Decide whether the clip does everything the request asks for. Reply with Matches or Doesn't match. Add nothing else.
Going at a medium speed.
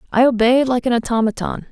Matches